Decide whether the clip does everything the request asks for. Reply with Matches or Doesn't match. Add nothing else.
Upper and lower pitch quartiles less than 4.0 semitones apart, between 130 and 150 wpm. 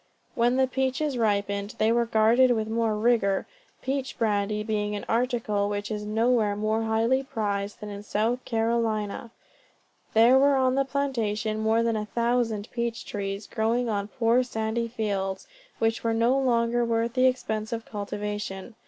Doesn't match